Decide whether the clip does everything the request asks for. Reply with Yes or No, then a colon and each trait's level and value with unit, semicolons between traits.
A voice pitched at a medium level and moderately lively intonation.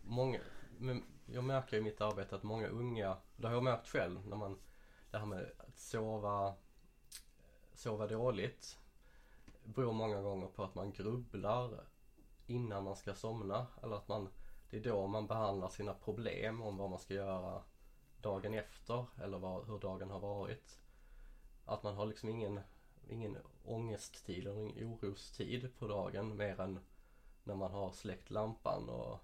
No: low, 105 Hz; average, 3.0 semitones